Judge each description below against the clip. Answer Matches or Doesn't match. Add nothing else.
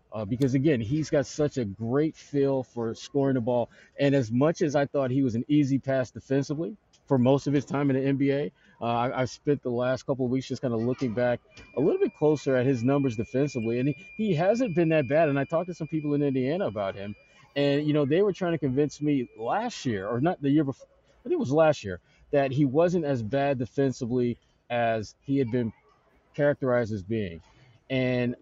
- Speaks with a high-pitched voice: Doesn't match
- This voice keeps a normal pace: Doesn't match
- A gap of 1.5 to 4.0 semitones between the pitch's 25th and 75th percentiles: Matches